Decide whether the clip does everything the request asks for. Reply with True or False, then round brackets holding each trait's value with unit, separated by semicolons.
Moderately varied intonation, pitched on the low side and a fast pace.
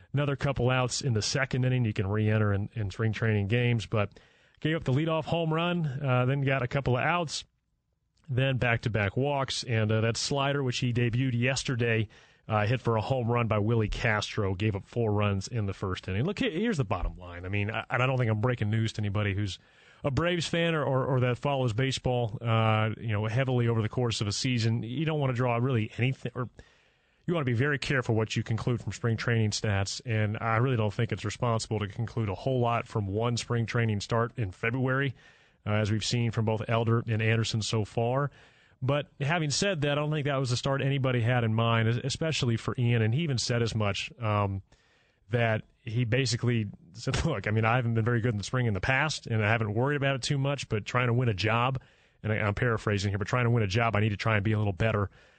True (3.2 semitones; 120 Hz; 240 wpm)